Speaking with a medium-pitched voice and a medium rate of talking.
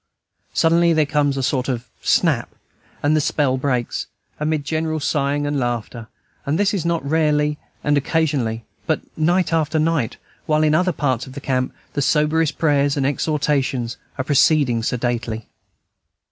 Yes: medium, 145 Hz; average, 150 wpm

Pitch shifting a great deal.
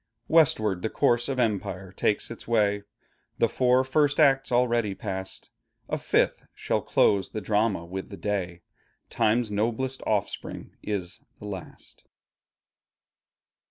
No: average, 4.0 semitones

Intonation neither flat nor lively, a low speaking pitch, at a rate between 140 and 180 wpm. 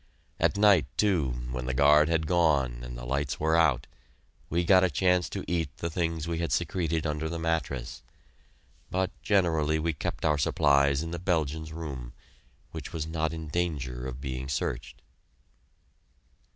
Yes: average, 3.4 semitones; very low, 80 Hz; average, 165 wpm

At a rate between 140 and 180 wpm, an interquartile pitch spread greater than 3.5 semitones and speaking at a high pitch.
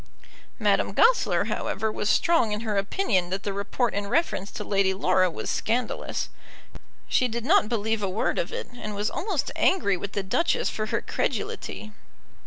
Yes: average, 175 wpm; average, 4.0 semitones; high, 215 Hz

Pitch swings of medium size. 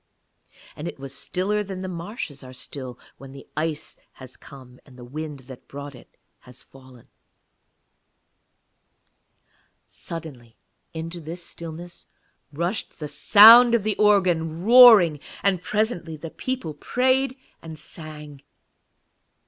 No: wide, 6.0 semitones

